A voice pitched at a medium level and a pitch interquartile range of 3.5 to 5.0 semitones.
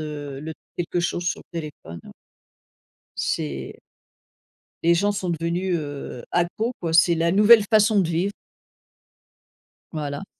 Yes: medium, 170 Hz; average, 3.9 semitones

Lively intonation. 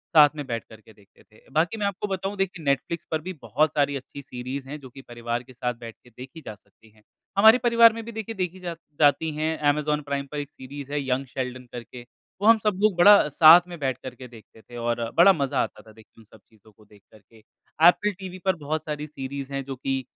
Yes: wide, 5.9 semitones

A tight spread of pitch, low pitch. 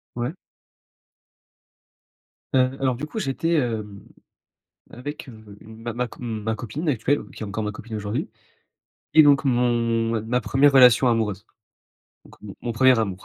No: average, 3.1 semitones; low, 120 Hz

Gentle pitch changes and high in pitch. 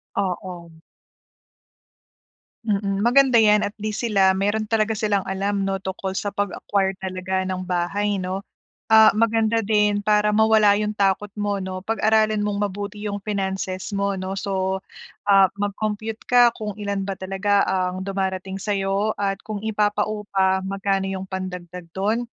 Yes: narrow, 1.7 semitones; high, 200 Hz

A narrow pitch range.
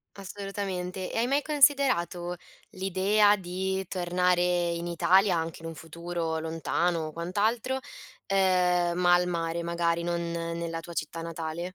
Yes: narrow, 2.1 semitones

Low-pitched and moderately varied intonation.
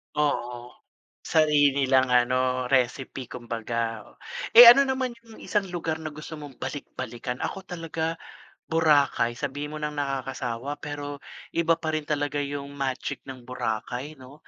No: medium, 145 Hz; average, 3.5 semitones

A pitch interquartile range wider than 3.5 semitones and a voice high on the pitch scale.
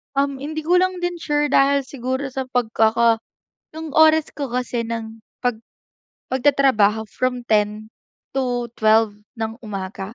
Yes: average, 4.1 semitones; very high, 250 Hz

